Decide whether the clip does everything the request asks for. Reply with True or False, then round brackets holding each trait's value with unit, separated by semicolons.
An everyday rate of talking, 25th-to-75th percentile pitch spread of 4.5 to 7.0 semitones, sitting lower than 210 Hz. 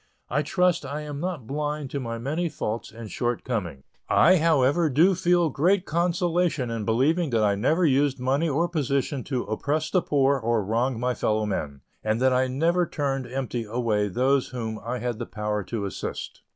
True (185 wpm; 5.1 semitones; 135 Hz)